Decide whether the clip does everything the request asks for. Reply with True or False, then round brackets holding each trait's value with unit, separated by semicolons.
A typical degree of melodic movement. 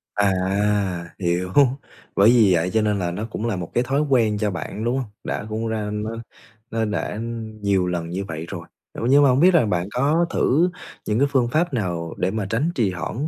True (4.9 semitones)